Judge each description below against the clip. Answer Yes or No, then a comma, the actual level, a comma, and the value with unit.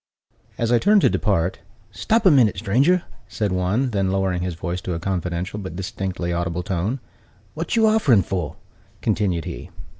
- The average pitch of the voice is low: Yes, very low, 95 Hz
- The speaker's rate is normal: Yes, average, 170 wpm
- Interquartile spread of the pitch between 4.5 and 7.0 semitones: Yes, average, 5.2 semitones